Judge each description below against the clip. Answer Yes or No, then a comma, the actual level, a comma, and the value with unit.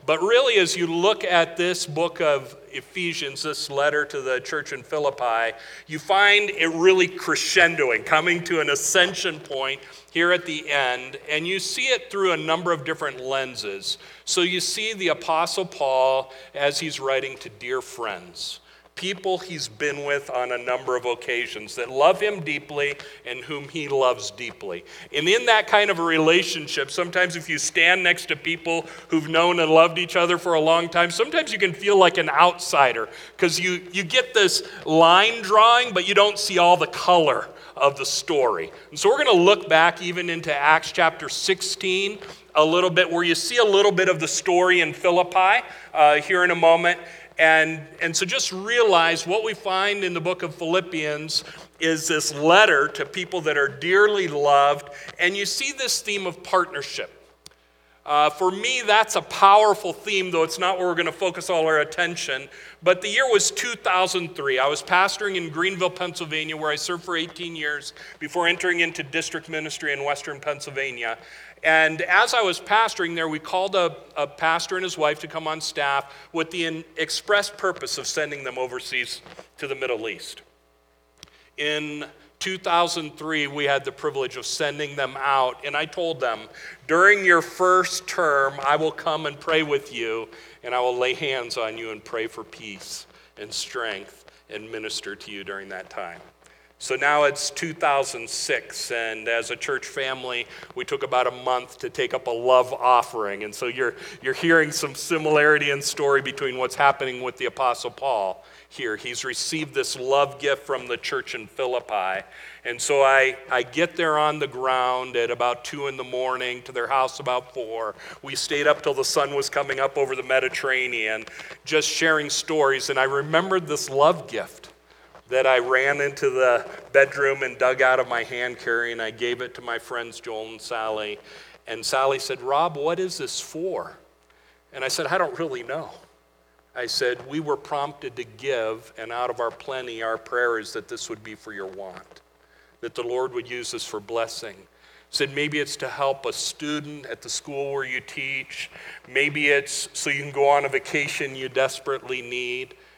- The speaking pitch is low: No, medium, 155 Hz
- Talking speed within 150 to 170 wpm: No, average, 190 wpm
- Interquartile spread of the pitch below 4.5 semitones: No, average, 5.2 semitones